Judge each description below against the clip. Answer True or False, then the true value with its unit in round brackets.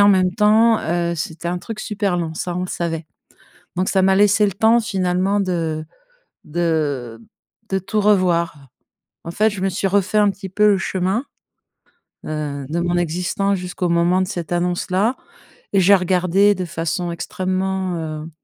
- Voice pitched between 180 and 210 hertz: True (185 Hz)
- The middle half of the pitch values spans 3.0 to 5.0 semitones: False (2.6 semitones)